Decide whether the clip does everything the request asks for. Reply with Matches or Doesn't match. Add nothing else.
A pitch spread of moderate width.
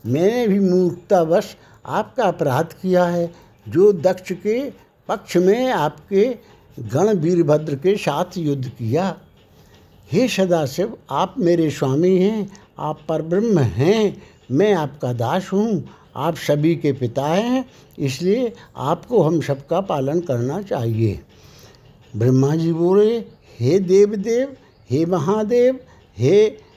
Doesn't match